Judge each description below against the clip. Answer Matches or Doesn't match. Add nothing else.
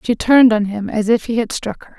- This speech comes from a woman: Matches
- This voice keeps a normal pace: Doesn't match